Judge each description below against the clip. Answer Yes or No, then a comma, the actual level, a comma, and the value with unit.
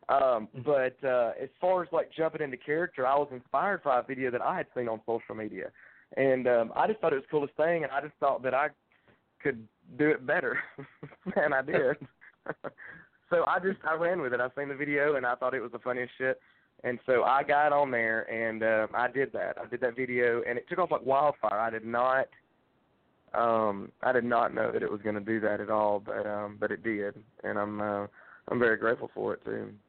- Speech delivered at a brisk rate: Yes, fast, 235 wpm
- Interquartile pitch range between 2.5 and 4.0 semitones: No, average, 4.8 semitones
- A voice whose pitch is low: Yes, low, 125 Hz